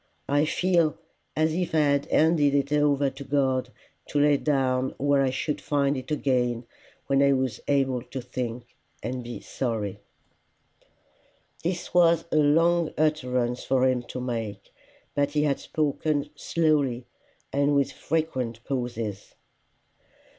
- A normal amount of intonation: Yes, average, 3.0 semitones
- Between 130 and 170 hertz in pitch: Yes, medium, 140 Hz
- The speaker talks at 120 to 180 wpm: Yes, average, 140 wpm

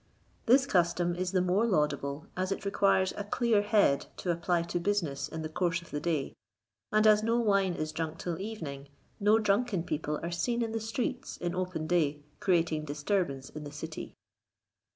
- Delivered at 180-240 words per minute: Yes, average, 185 wpm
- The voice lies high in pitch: No, medium, 175 Hz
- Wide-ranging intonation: No, average, 4.7 semitones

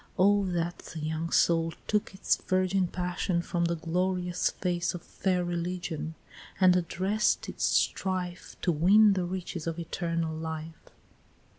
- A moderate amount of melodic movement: No, narrow, 1.9 semitones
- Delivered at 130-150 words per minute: Yes, average, 140 wpm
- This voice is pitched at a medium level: Yes, medium, 175 Hz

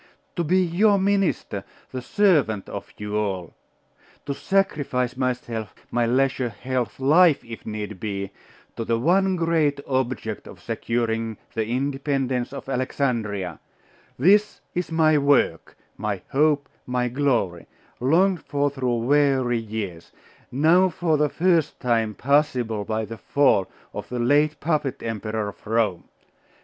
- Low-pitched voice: Yes, low, 130 Hz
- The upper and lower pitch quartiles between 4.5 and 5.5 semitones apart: Yes, average, 5.1 semitones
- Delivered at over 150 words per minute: No, slow, 135 wpm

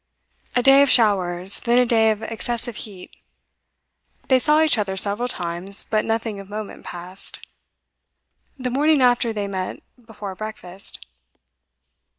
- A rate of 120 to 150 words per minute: Yes, average, 140 wpm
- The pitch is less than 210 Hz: No, high, 215 Hz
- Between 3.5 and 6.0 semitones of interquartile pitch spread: Yes, average, 3.9 semitones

